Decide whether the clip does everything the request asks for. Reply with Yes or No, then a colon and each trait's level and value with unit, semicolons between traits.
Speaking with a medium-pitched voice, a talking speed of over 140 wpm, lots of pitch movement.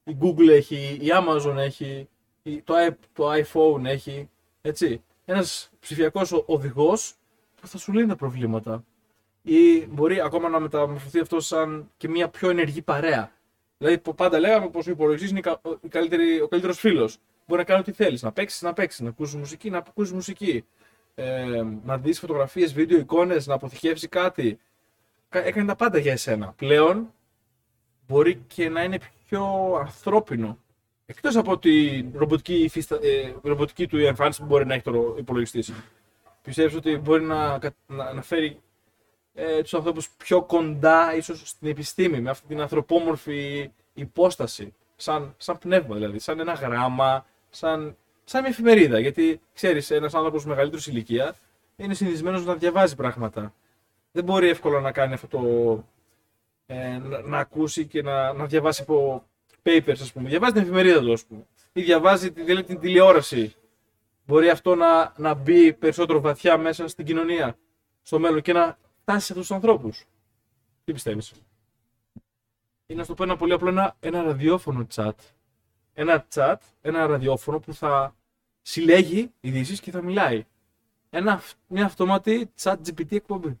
Yes: medium, 150 Hz; average, 150 wpm; wide, 6.8 semitones